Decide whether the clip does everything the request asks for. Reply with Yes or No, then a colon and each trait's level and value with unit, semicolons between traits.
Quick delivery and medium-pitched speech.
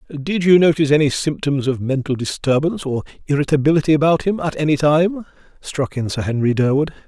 No: average, 170 wpm; medium, 145 Hz